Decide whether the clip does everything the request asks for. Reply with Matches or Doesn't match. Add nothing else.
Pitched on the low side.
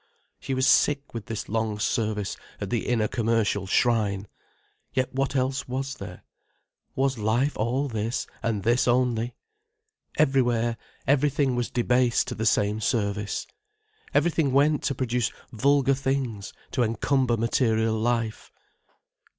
Matches